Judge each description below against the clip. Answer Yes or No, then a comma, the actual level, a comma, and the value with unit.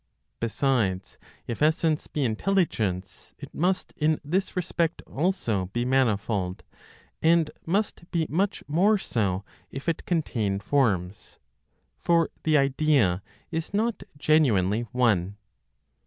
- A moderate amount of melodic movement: No, wide, 8.1 semitones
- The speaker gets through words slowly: Yes, slow, 110 wpm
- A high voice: No, medium, 140 Hz